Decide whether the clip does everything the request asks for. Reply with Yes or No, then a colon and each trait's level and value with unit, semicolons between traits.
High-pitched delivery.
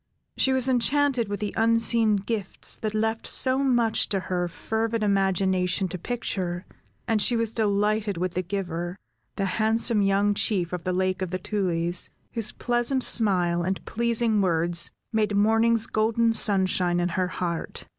Yes: high, 205 Hz